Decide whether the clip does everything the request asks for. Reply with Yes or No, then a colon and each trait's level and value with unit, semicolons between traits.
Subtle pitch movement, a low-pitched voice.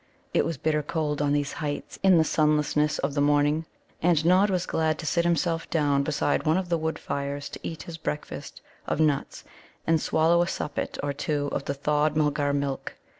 No: narrow, 2.1 semitones; medium, 150 Hz